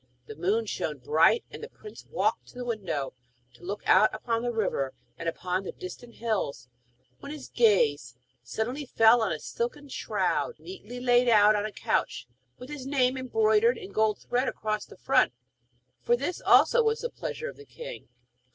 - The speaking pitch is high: Yes, high, 245 Hz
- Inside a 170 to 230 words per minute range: Yes, average, 180 wpm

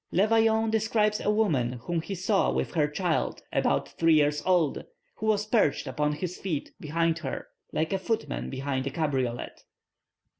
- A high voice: No, medium, 170 Hz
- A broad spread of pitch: Yes, wide, 6.1 semitones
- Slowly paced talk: No, average, 165 wpm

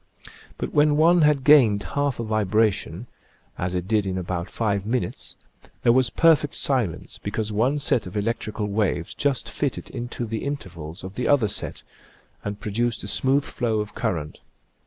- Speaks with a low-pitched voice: Yes, low, 110 Hz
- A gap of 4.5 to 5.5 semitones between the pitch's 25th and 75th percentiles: Yes, average, 4.9 semitones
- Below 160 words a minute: No, average, 165 wpm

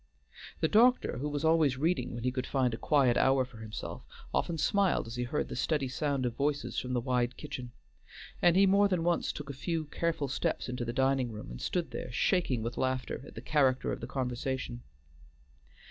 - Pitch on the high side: No, low, 135 Hz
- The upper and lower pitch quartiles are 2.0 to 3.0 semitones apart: No, average, 4.3 semitones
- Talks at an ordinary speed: No, fast, 210 wpm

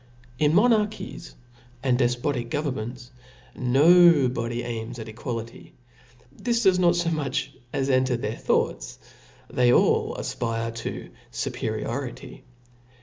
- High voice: No, low, 130 Hz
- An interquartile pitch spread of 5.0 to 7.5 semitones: Yes, wide, 5.4 semitones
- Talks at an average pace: No, slow, 110 wpm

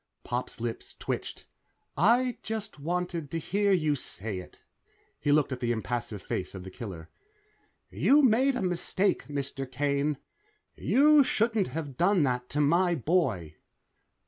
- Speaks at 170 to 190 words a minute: No, average, 145 wpm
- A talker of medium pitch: Yes, medium, 150 Hz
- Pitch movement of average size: No, wide, 8.1 semitones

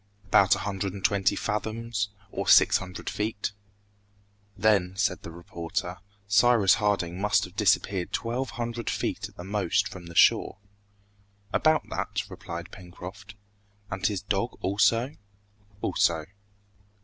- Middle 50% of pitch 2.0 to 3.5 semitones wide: Yes, average, 2.8 semitones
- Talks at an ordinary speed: No, slow, 130 wpm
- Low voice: Yes, low, 100 Hz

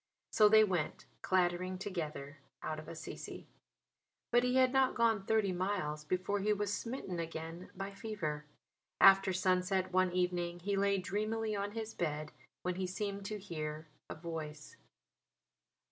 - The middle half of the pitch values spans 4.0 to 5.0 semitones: No, average, 3.4 semitones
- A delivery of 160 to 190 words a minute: No, average, 145 wpm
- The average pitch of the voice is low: No, medium, 185 Hz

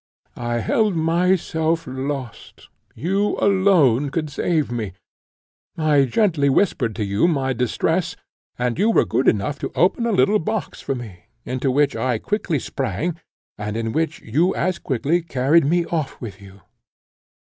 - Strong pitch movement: Yes, wide, 6.0 semitones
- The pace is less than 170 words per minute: Yes, average, 150 wpm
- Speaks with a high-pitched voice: No, medium, 145 Hz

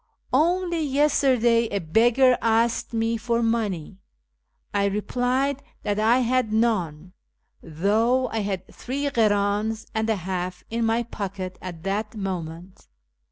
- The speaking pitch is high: Yes, high, 220 Hz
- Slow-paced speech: Yes, slow, 125 wpm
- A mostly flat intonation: No, average, 3.7 semitones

